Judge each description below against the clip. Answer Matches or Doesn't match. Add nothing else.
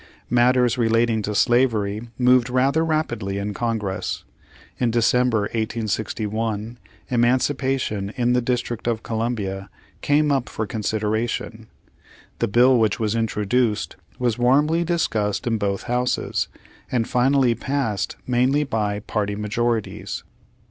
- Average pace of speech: Doesn't match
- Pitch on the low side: Matches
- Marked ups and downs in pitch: Doesn't match